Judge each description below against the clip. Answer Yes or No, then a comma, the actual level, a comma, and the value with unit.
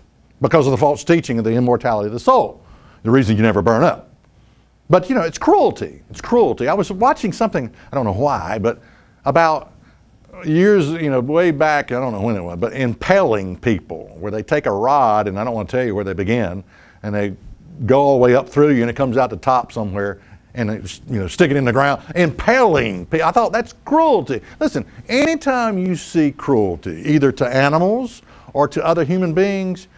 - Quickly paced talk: Yes, fast, 215 wpm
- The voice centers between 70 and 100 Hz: No, low, 135 Hz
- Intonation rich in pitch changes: Yes, wide, 7.4 semitones